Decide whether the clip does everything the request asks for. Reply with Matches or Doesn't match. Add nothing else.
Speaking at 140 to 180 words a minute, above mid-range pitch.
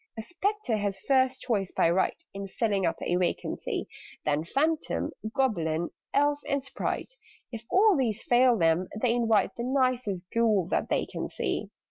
Matches